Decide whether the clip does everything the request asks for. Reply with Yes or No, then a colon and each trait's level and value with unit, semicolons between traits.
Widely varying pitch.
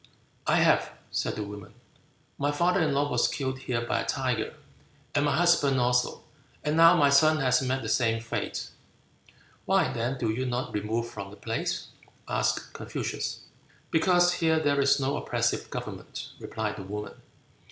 No: average, 4.0 semitones